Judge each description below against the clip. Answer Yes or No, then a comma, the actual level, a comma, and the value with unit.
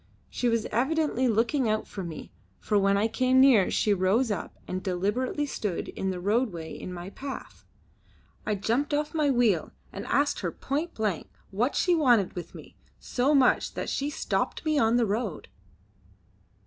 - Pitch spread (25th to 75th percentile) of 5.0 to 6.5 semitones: Yes, wide, 5.4 semitones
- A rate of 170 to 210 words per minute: Yes, average, 175 wpm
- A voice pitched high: Yes, high, 230 Hz